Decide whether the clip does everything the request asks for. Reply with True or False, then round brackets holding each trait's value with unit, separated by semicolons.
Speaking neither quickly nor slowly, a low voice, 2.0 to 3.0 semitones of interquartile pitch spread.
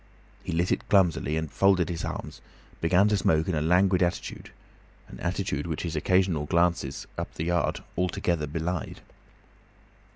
True (155 wpm; 85 Hz; 2.4 semitones)